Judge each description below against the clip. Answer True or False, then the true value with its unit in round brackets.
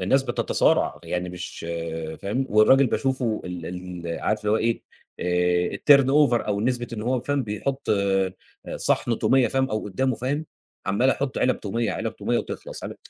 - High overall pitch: False (115 Hz)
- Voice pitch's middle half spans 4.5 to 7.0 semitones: True (5.0 semitones)